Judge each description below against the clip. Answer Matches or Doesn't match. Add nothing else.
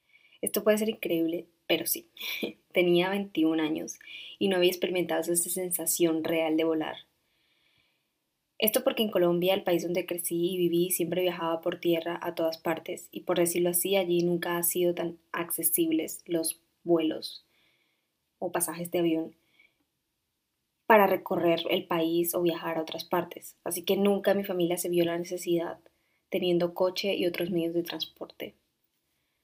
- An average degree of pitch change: Doesn't match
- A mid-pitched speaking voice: Matches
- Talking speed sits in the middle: Matches